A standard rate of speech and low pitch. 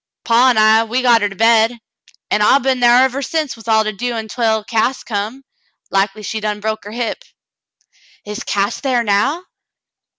No: average, 185 wpm; high, 225 Hz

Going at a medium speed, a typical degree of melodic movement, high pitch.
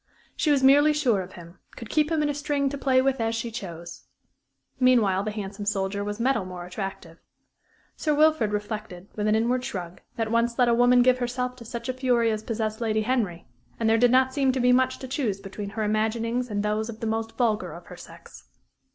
No: fast, 220 wpm; average, 3.6 semitones; high, 230 Hz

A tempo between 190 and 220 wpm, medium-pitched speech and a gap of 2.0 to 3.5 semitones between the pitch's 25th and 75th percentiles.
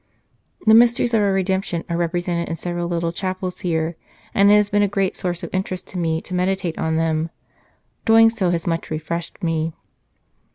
Yes: average, 200 wpm; medium, 175 Hz; narrow, 2.6 semitones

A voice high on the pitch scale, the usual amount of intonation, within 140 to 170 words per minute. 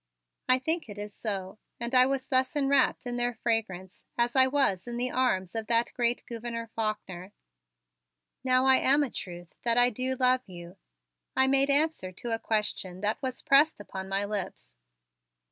No: high, 235 Hz; average, 4.2 semitones; average, 180 wpm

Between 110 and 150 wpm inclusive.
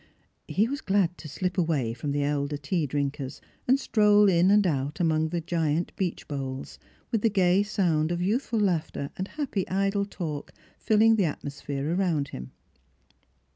No: average, 165 wpm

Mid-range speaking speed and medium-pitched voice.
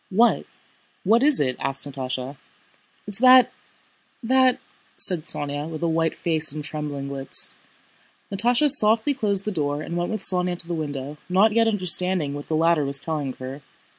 Yes: average, 165 wpm; medium, 165 Hz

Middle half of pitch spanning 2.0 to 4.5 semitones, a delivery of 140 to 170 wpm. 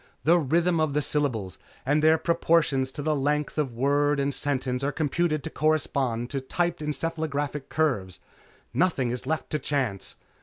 Yes: average, 3.0 semitones; average, 160 wpm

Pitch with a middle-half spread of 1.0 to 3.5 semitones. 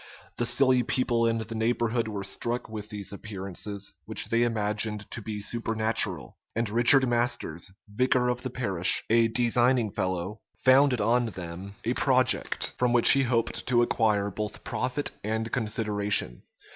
Yes: average, 2.8 semitones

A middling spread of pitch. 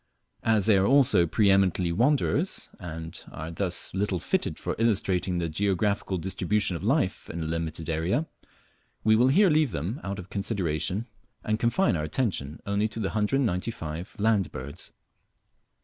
Yes: average, 4.8 semitones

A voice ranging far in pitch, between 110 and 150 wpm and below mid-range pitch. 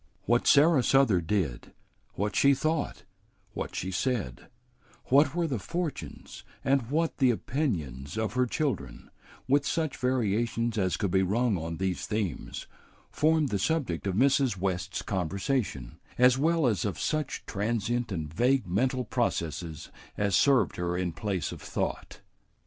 Yes: wide, 6.6 semitones; average, 145 wpm; low, 115 Hz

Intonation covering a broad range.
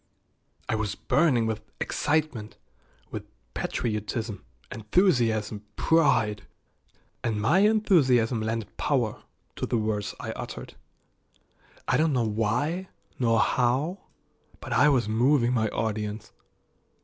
No: average, 5.0 semitones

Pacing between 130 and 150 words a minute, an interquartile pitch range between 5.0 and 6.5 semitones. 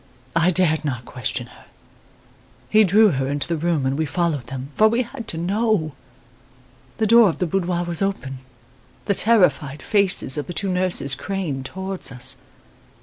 No: average, 170 wpm; wide, 5.6 semitones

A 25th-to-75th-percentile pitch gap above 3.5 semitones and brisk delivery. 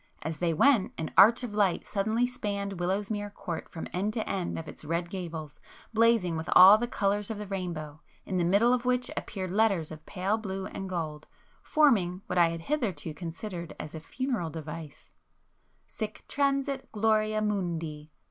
No: average, 4.6 semitones; average, 180 wpm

